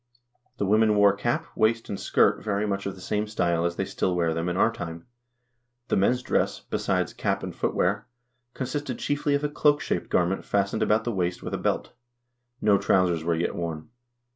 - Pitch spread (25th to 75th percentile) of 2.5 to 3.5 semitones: No, average, 4.2 semitones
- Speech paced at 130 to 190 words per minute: No, average, 200 wpm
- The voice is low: Yes, low, 100 Hz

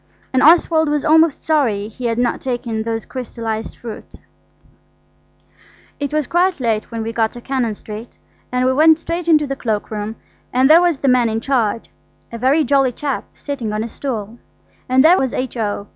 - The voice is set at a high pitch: Yes, very high, 255 Hz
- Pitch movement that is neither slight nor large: Yes, average, 4.5 semitones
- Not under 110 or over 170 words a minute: No, average, 185 wpm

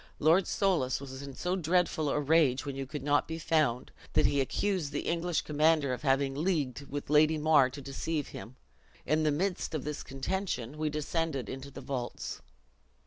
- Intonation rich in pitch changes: No, average, 3.0 semitones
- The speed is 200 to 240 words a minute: No, average, 185 wpm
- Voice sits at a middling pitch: Yes, medium, 150 Hz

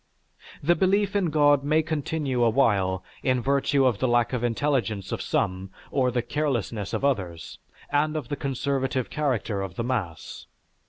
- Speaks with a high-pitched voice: No, low, 130 Hz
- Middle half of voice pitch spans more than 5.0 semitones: No, average, 4.4 semitones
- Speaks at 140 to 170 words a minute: Yes, average, 160 wpm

